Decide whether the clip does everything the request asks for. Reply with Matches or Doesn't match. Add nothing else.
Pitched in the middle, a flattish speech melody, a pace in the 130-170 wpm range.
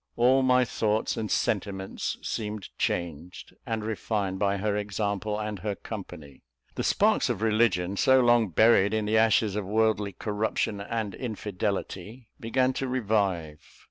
Doesn't match